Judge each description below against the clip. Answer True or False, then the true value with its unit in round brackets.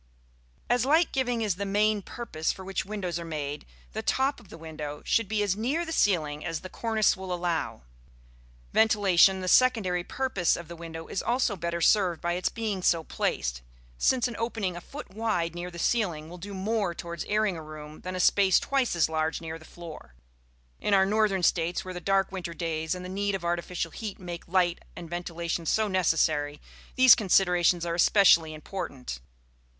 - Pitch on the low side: False (180 Hz)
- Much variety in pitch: False (3.8 semitones)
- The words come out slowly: False (190 wpm)